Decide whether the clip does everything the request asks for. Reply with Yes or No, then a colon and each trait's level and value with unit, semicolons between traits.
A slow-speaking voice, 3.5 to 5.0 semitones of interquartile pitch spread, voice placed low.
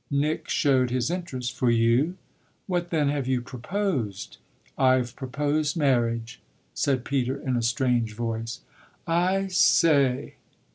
Yes: slow, 125 wpm; average, 4.1 semitones; low, 130 Hz